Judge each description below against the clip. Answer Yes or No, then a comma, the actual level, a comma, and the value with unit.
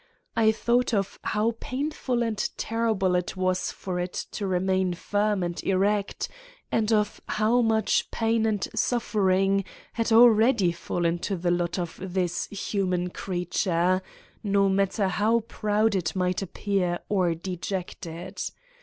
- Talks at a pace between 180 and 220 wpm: No, slow, 135 wpm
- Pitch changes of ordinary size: Yes, average, 3.3 semitones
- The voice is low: No, high, 195 Hz